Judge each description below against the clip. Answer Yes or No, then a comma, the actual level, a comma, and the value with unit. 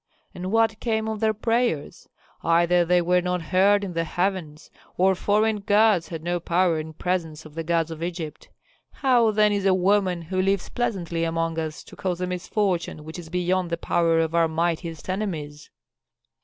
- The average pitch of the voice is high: No, medium, 180 Hz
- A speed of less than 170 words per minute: No, average, 185 wpm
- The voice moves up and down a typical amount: Yes, average, 3.3 semitones